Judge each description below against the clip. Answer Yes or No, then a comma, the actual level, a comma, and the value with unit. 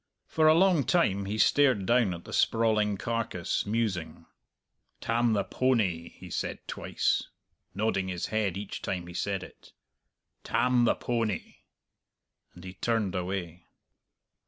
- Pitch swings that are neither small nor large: Yes, average, 4.0 semitones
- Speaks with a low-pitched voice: Yes, low, 105 Hz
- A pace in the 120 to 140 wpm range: Yes, slow, 135 wpm